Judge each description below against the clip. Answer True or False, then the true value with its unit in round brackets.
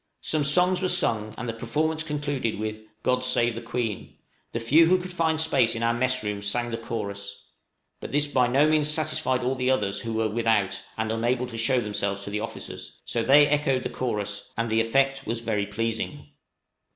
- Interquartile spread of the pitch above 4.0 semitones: True (4.5 semitones)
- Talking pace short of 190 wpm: False (200 wpm)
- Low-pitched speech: True (120 Hz)